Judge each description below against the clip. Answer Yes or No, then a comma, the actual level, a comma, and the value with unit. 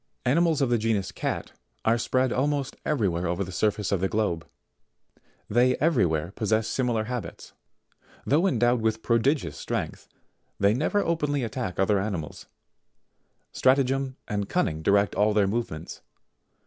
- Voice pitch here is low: Yes, low, 110 Hz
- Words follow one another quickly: No, average, 150 wpm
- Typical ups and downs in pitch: Yes, average, 4.9 semitones